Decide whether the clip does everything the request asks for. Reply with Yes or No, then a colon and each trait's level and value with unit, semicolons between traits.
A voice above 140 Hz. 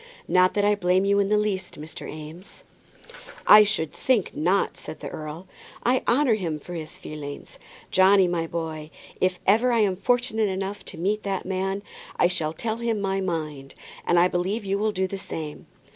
Yes: high, 190 Hz